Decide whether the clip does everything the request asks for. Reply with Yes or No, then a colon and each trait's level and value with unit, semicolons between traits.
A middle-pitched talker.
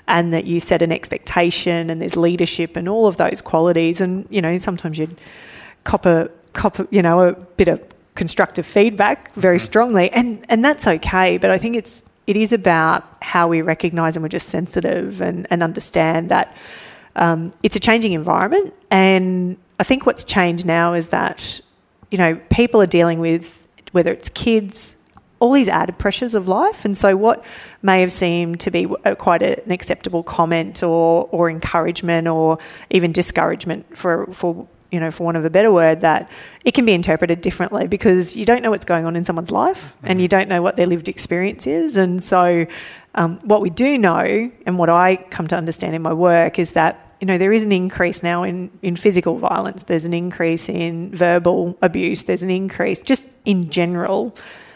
Yes: medium, 180 Hz